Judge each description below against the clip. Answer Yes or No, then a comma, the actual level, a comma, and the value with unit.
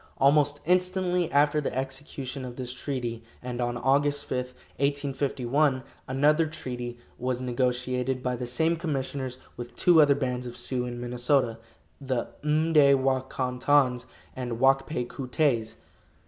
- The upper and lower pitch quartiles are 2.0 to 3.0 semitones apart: Yes, narrow, 2.6 semitones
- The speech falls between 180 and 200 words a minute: No, average, 145 wpm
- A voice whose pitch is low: Yes, low, 130 Hz